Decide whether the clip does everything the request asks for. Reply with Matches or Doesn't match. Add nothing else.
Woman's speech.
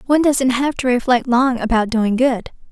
Matches